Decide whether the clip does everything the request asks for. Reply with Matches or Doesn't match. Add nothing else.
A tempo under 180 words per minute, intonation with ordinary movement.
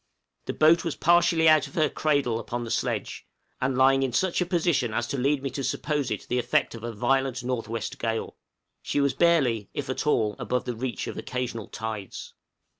Doesn't match